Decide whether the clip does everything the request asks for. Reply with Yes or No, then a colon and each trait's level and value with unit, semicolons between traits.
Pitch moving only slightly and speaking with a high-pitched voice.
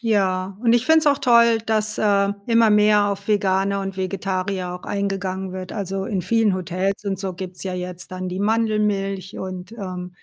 Yes: narrow, 2.3 semitones; high, 195 Hz